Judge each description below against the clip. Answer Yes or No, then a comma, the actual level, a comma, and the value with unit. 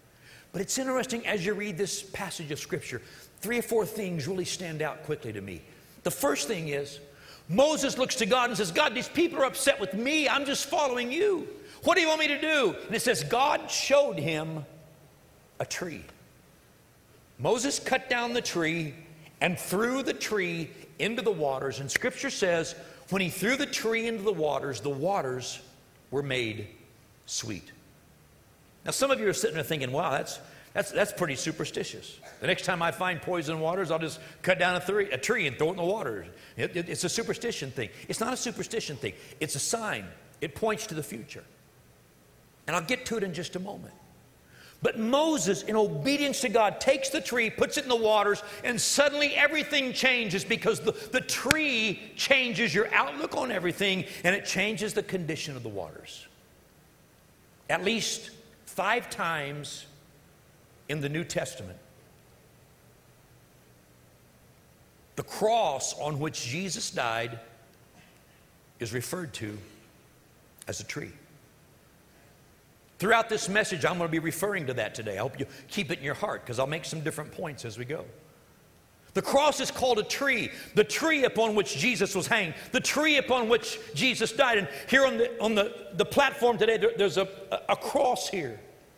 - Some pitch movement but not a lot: No, wide, 7.7 semitones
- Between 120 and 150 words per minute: No, average, 180 wpm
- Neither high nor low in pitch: No, high, 195 Hz